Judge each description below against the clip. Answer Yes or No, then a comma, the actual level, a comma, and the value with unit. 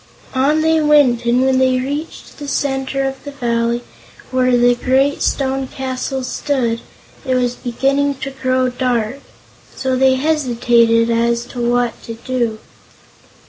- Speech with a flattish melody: Yes, narrow, 2.1 semitones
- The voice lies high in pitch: Yes, very high, 255 Hz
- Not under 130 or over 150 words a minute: Yes, average, 140 wpm